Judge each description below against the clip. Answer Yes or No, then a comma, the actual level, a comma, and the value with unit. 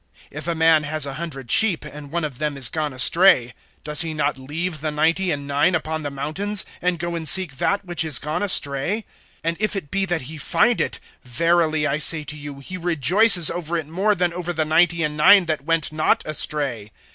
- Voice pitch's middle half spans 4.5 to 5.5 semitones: No, average, 3.1 semitones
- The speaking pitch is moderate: Yes, medium, 155 Hz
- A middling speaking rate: No, fast, 215 wpm